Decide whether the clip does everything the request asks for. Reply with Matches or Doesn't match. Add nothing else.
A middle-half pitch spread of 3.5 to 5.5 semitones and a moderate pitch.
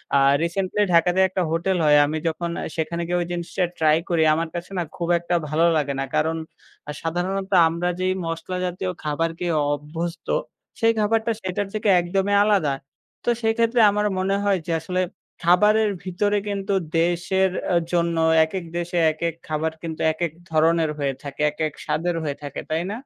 Doesn't match